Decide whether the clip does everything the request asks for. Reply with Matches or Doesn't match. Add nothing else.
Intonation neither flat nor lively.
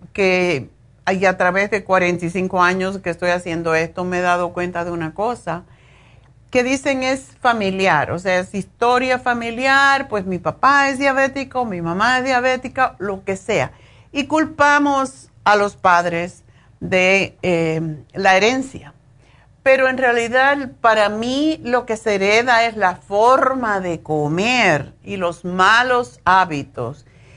Doesn't match